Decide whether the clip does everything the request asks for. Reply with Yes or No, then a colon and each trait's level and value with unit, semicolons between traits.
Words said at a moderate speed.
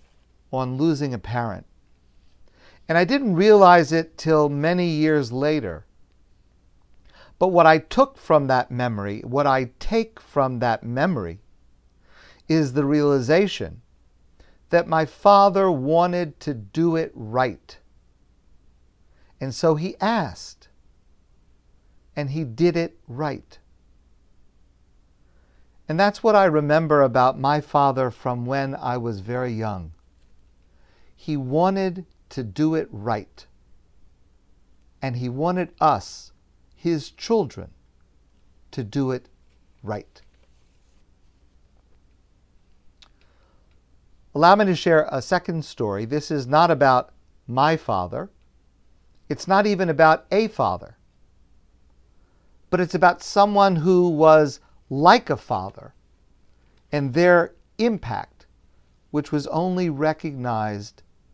No: slow, 110 wpm